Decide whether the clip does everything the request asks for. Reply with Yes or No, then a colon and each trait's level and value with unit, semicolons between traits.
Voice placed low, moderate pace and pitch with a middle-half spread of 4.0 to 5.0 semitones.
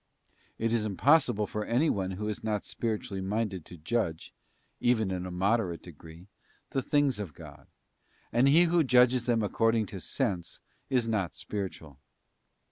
Yes: low, 105 Hz; average, 155 wpm; average, 4.3 semitones